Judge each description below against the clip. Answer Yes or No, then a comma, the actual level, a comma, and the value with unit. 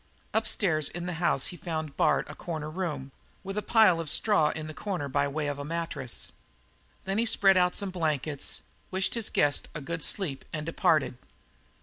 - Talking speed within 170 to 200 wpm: Yes, average, 190 wpm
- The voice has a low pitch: No, medium, 165 Hz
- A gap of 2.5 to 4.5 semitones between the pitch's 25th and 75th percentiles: Yes, average, 4.0 semitones